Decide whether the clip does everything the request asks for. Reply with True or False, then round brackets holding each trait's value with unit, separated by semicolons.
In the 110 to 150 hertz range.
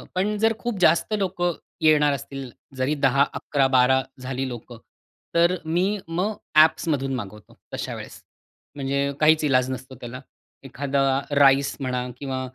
True (140 Hz)